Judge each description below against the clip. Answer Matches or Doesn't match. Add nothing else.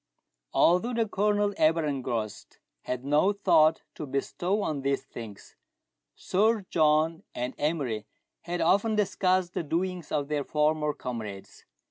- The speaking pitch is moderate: Matches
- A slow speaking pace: Matches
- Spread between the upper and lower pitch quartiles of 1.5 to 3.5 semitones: Doesn't match